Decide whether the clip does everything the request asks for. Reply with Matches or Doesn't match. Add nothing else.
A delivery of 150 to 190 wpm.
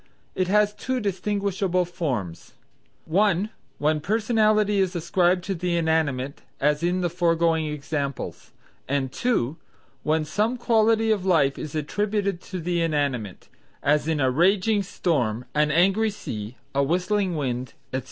Doesn't match